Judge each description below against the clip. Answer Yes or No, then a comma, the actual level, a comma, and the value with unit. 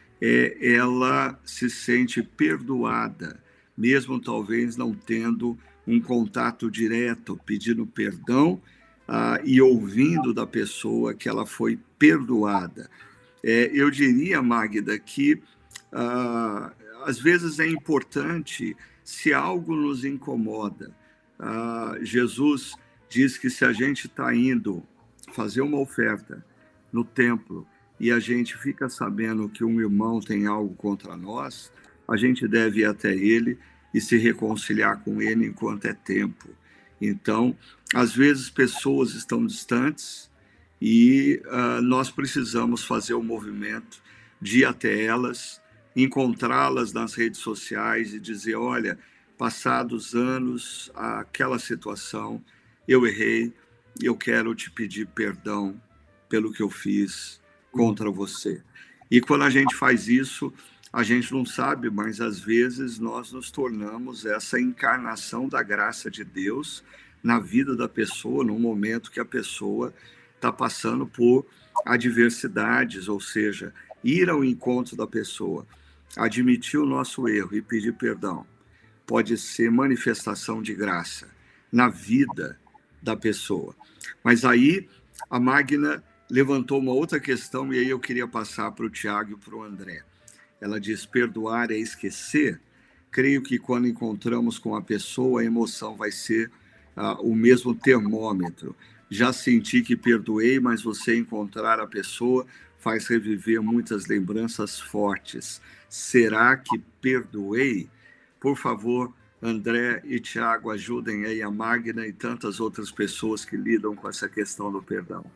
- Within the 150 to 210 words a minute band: No, average, 135 wpm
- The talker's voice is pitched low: Yes, low, 115 Hz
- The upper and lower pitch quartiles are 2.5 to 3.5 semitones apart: Yes, average, 2.8 semitones